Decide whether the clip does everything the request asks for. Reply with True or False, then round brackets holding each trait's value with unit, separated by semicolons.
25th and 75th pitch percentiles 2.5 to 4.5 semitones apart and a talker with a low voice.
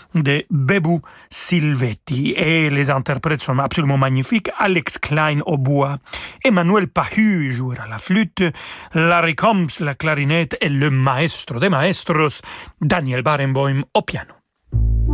False (3.9 semitones; 150 Hz)